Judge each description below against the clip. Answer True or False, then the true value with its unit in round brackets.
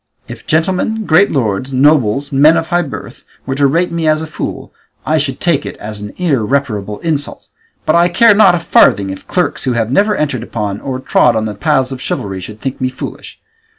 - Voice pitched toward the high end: False (140 Hz)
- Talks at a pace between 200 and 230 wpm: True (205 wpm)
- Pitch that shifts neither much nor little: False (5.8 semitones)